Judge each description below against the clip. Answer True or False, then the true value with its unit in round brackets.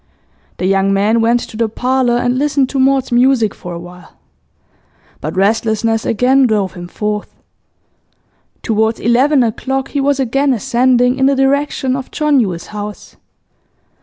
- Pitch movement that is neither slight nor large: True (4.1 semitones)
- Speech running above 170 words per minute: False (145 wpm)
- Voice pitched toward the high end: True (240 Hz)